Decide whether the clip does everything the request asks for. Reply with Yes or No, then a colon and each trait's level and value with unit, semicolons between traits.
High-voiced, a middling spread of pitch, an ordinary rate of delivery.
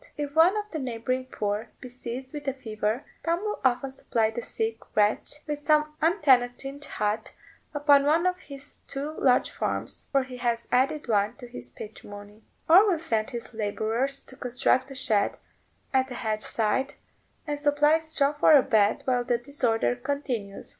Yes: very high, 260 Hz; average, 4.4 semitones; average, 175 wpm